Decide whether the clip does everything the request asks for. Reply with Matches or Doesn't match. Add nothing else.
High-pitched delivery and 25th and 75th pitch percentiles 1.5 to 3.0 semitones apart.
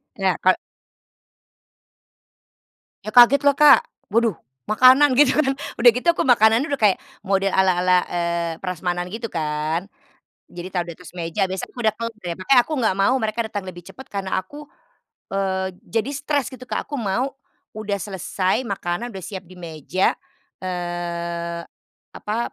Doesn't match